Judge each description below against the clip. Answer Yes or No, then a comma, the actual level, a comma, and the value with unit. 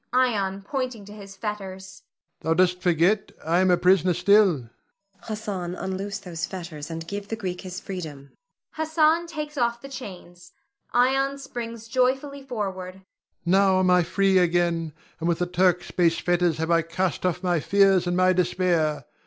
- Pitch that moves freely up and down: No, average, 3.4 semitones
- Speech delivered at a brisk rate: No, average, 170 wpm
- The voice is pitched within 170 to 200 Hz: Yes, medium, 185 Hz